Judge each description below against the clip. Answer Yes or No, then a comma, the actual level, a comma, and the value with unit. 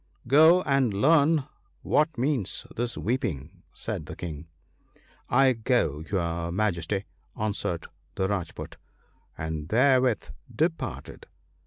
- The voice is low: Yes, low, 110 Hz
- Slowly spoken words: Yes, slow, 115 wpm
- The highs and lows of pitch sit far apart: Yes, wide, 7.8 semitones